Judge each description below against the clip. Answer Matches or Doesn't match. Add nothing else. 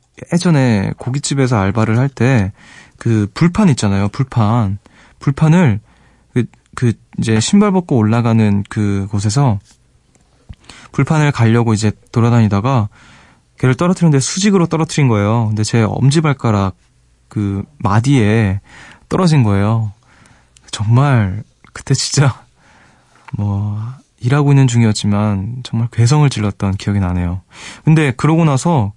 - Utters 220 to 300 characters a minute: Matches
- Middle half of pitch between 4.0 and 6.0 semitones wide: Matches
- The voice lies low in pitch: Matches